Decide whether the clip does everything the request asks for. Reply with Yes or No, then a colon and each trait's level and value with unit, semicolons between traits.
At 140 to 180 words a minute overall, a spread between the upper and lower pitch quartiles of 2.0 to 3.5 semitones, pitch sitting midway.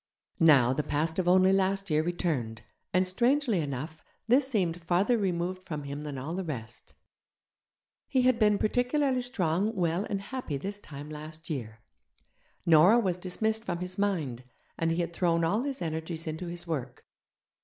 No: average, 165 wpm; average, 4.5 semitones; medium, 175 Hz